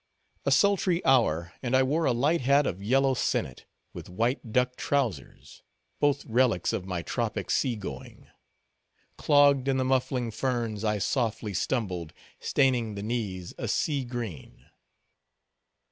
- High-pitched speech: No, low, 120 Hz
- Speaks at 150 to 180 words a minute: No, slow, 135 wpm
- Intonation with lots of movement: No, average, 4.4 semitones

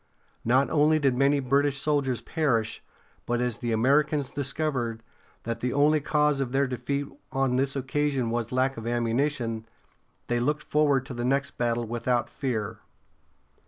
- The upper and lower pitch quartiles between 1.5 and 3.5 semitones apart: Yes, average, 3.0 semitones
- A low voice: Yes, low, 130 Hz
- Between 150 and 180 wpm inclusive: Yes, average, 155 wpm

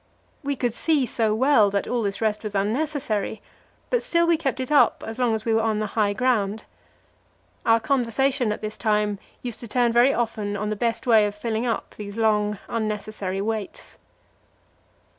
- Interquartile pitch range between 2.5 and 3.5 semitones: Yes, average, 2.9 semitones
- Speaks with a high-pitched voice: Yes, high, 225 Hz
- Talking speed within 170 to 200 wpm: Yes, average, 185 wpm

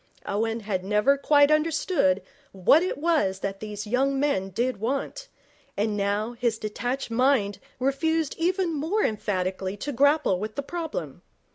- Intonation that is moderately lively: No, wide, 6.2 semitones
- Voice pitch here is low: No, high, 245 Hz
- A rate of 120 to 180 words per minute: Yes, average, 145 wpm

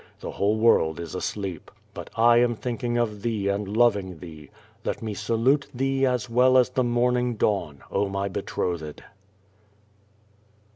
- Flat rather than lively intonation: No, average, 3.9 semitones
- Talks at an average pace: Yes, average, 155 wpm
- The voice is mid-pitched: No, low, 110 Hz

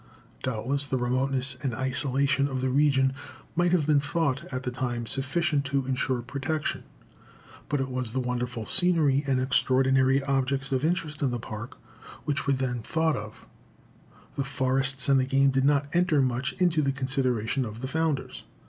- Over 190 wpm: No, average, 170 wpm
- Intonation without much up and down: Yes, narrow, 1.8 semitones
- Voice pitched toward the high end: No, low, 135 Hz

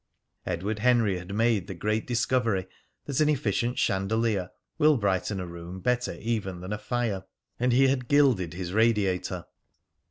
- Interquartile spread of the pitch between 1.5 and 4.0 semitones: No, average, 4.5 semitones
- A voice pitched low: Yes, low, 105 Hz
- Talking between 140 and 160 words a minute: Yes, average, 155 wpm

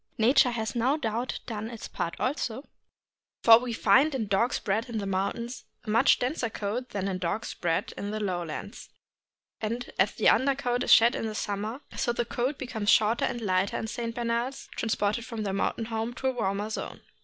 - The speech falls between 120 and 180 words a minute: No, average, 200 wpm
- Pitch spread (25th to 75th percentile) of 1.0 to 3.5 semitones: Yes, average, 2.8 semitones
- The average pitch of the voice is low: No, high, 225 Hz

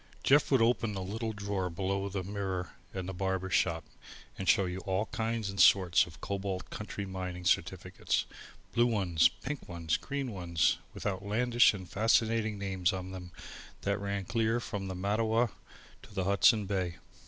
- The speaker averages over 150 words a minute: Yes, average, 165 wpm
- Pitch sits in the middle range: No, low, 100 Hz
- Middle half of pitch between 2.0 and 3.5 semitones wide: Yes, average, 3.0 semitones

